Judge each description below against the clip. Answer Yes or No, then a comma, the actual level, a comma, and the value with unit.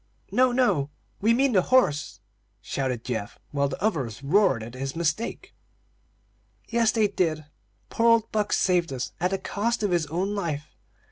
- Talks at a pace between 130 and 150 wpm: No, average, 160 wpm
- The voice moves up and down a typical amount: No, wide, 7.4 semitones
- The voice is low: No, medium, 180 Hz